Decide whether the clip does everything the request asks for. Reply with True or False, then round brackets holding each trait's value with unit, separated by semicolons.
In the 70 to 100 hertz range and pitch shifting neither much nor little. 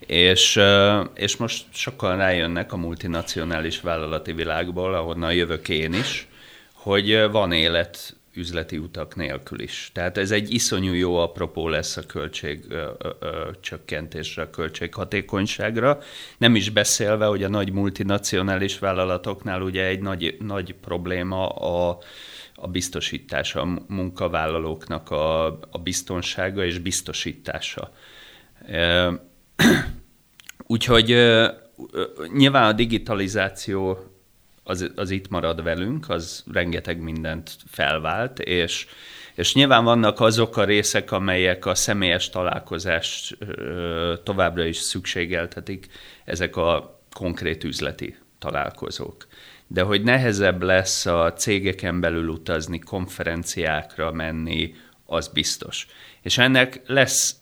True (95 Hz; 3.4 semitones)